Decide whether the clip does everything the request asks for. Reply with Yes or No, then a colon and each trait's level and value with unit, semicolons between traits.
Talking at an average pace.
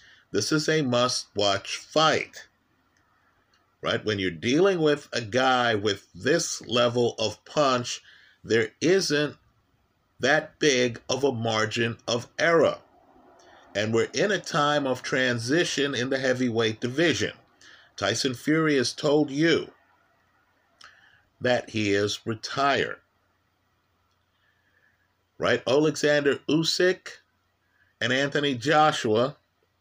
No: slow, 105 wpm